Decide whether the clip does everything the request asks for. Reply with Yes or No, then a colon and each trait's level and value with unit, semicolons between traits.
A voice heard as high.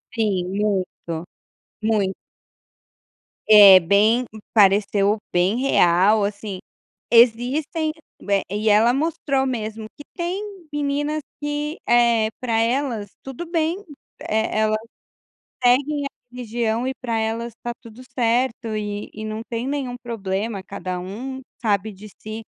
Yes: high, 225 Hz